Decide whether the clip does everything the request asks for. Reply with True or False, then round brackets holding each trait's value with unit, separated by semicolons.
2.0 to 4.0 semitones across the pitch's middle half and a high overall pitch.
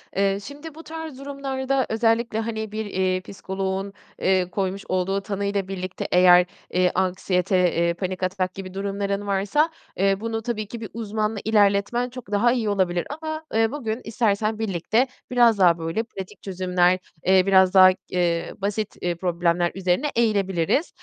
True (3.3 semitones; 200 Hz)